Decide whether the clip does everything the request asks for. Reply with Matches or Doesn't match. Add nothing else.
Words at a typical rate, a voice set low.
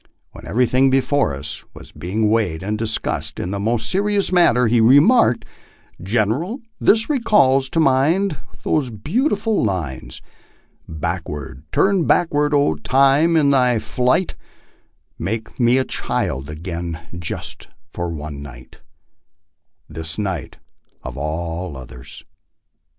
Doesn't match